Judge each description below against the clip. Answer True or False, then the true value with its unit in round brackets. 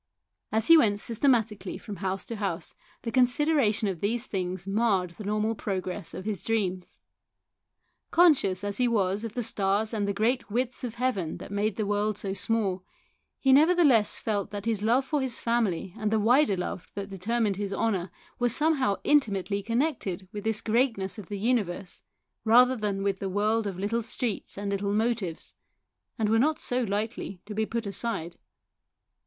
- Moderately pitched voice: False (215 Hz)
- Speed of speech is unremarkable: True (180 wpm)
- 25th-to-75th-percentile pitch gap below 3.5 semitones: True (3.1 semitones)